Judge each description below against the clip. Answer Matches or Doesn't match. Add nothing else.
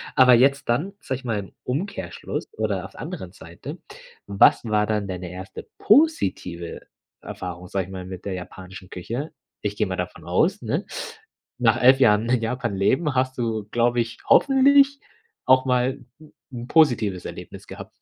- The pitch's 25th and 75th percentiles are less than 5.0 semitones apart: Doesn't match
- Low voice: Matches